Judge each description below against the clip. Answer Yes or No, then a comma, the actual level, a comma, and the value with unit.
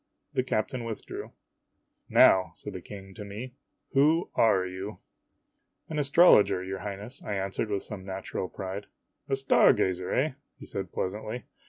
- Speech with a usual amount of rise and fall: Yes, average, 4.7 semitones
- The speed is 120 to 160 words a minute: No, average, 170 wpm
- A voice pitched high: No, low, 105 Hz